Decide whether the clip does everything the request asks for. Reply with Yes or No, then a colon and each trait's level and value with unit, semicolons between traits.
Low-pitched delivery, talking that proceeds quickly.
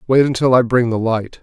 Yes: low, 120 Hz; fast, 250 wpm